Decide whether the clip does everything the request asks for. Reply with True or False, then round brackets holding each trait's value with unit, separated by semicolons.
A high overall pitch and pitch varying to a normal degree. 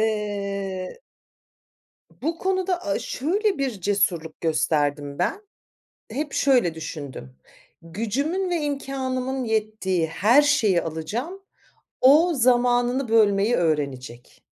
False (220 Hz; 8.0 semitones)